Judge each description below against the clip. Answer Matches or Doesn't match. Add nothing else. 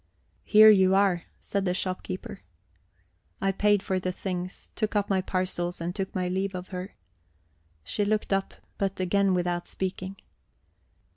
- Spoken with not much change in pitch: Matches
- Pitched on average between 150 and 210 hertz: Matches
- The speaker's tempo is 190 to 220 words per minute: Doesn't match